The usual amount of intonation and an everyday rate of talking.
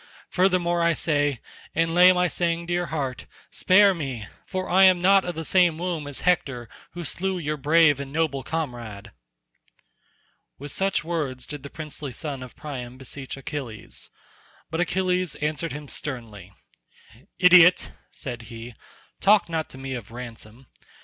Yes: average, 5.0 semitones; average, 155 wpm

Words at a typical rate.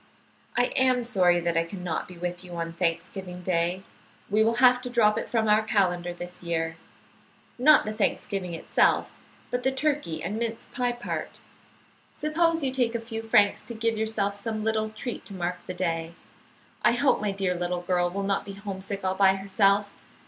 Yes: average, 190 wpm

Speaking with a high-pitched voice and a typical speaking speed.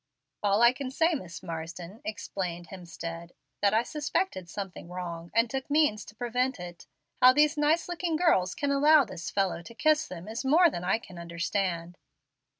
Yes: high, 210 Hz; average, 180 wpm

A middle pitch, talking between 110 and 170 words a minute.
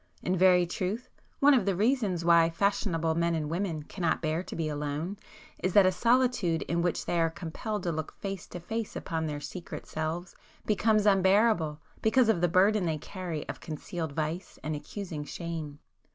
No: medium, 175 Hz; average, 180 wpm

